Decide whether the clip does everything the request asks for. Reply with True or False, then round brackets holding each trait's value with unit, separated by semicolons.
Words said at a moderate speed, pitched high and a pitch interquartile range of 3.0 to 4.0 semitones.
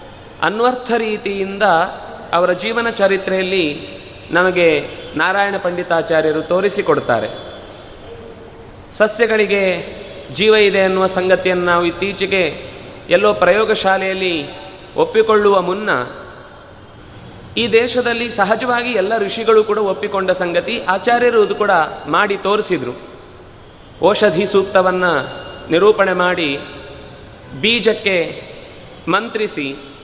True (75 wpm; 195 Hz; 3.3 semitones)